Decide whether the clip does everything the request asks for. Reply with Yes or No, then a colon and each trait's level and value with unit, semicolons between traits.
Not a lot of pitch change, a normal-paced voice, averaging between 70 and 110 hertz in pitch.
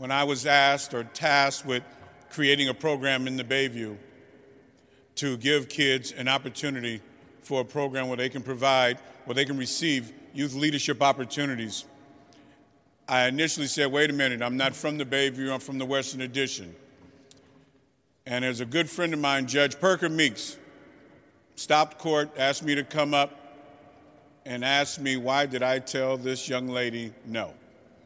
No: narrow, 1.6 semitones; average, 165 wpm; low, 135 Hz